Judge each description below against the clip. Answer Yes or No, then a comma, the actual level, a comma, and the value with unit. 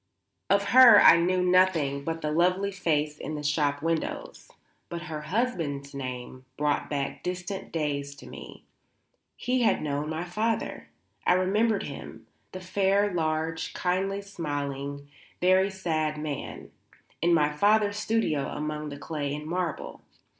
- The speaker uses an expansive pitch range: No, average, 4.2 semitones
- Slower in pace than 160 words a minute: Yes, average, 140 wpm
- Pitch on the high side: No, medium, 165 Hz